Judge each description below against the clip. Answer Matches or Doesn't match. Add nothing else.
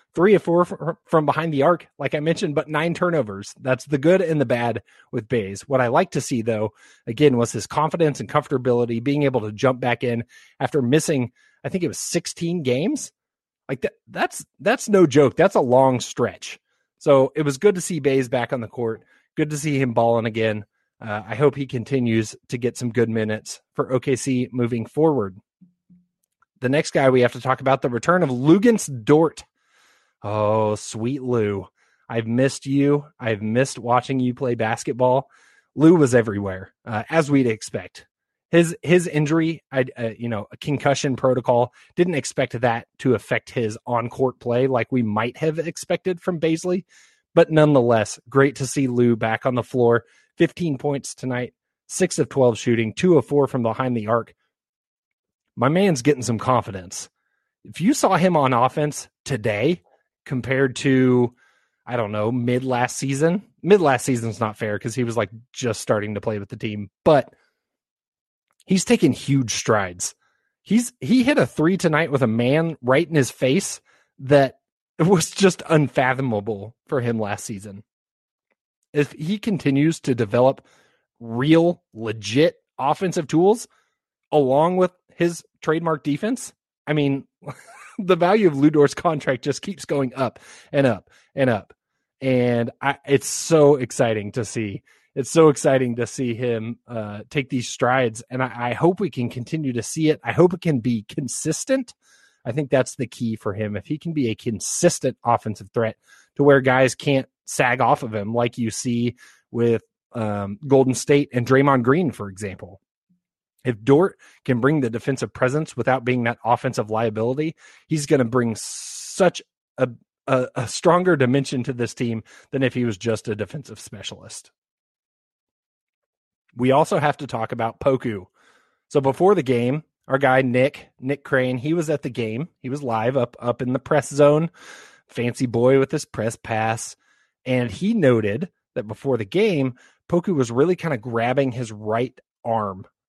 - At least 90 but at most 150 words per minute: Doesn't match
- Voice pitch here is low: Matches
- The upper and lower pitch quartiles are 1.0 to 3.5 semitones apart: Doesn't match